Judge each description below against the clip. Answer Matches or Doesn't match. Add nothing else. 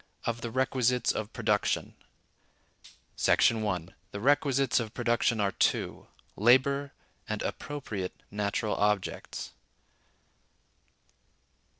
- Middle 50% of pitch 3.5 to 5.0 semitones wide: Matches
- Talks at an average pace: Doesn't match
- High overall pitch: Doesn't match